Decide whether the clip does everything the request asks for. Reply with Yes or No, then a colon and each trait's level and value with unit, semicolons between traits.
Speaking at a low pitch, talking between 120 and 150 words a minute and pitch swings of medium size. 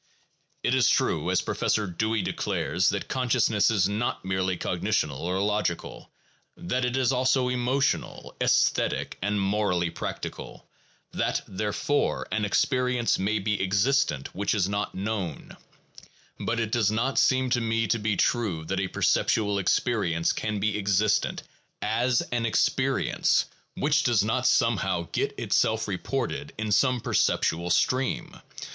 Yes: low, 105 Hz; average, 140 wpm; average, 4.0 semitones